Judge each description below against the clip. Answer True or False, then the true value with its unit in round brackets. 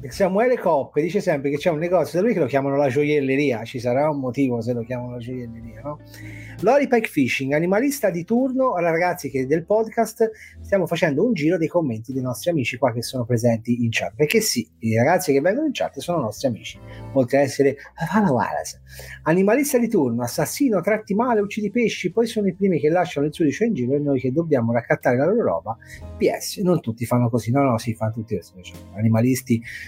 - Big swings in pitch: True (7.6 semitones)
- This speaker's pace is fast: True (205 wpm)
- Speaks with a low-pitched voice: False (145 Hz)